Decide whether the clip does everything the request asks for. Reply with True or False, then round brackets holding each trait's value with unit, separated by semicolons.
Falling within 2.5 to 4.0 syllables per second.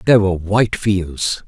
False (4.9 syllables/s)